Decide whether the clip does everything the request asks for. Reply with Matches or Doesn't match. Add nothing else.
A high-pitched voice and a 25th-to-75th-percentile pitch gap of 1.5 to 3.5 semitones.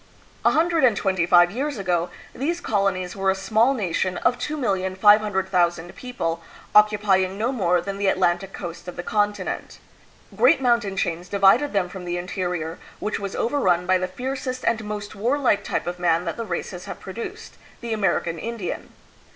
Doesn't match